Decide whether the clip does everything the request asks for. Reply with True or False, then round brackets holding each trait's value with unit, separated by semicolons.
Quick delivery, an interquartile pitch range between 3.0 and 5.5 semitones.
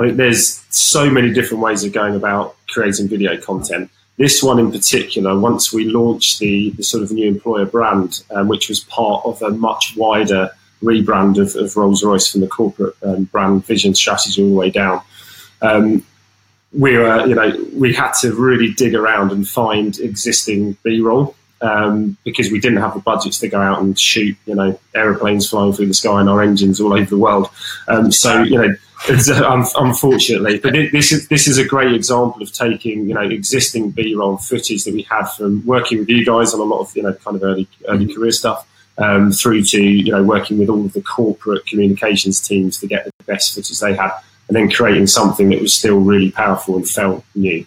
False (210 wpm; 2.6 semitones)